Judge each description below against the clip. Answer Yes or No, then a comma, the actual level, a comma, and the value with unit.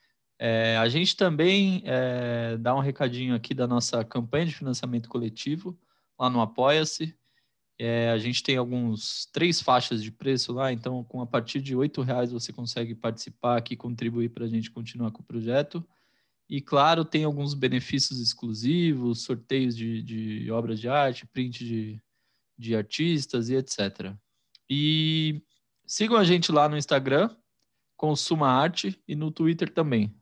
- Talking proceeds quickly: No, average, 155 wpm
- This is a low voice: Yes, low, 125 Hz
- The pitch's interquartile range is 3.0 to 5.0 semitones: Yes, average, 4.1 semitones